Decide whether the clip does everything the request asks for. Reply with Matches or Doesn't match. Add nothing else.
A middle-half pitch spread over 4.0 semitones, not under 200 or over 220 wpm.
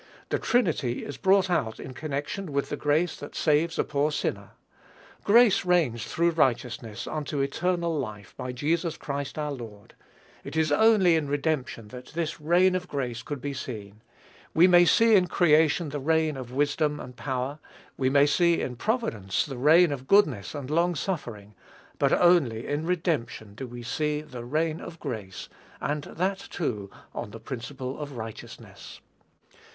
Doesn't match